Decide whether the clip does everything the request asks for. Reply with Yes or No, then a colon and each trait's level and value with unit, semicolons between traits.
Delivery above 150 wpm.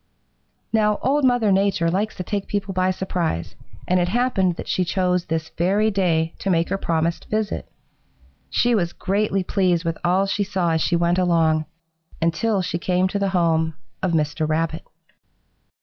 Yes: average, 170 wpm